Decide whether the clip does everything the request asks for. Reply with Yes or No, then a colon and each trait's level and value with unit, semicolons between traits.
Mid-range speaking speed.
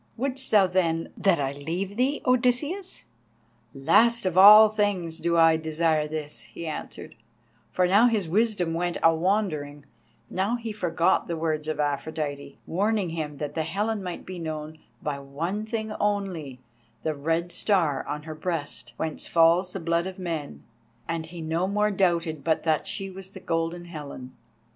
Yes: average, 165 wpm